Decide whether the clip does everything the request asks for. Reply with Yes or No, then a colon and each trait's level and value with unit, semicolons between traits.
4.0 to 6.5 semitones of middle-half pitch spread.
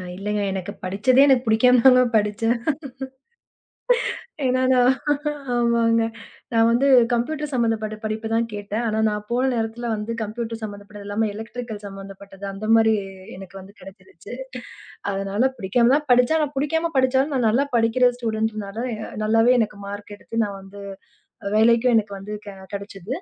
No: average, 3.2 semitones